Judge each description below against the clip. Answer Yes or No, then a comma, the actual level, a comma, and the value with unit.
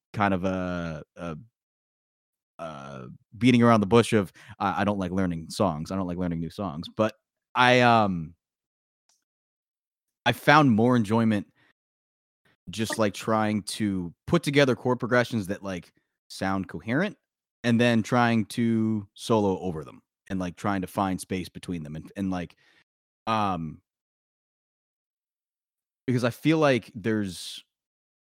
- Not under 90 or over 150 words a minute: Yes, average, 140 wpm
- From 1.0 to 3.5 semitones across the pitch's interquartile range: No, average, 4.3 semitones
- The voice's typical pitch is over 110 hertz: No, low, 105 Hz